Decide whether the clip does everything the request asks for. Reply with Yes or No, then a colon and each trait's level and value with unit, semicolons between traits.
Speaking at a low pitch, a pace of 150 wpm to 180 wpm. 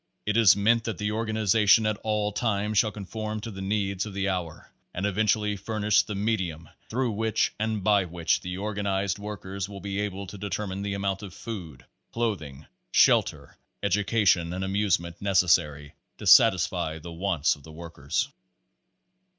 Yes: low, 100 Hz; average, 165 wpm